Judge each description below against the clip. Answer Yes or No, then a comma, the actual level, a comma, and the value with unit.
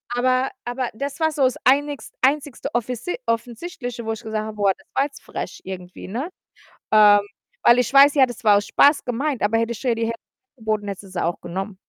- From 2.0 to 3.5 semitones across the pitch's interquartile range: No, average, 4.1 semitones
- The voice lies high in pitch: Yes, high, 240 Hz